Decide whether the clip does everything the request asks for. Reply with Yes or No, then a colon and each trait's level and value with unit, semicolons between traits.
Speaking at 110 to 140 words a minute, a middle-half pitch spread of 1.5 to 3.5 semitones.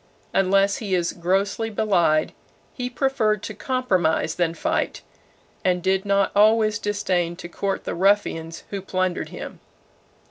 Yes: slow, 135 wpm; average, 3.2 semitones